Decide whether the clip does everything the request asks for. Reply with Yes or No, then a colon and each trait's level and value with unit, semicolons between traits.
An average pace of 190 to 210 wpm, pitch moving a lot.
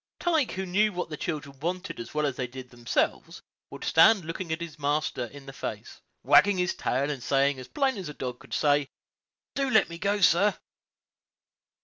Yes: average, 195 wpm; wide, 5.7 semitones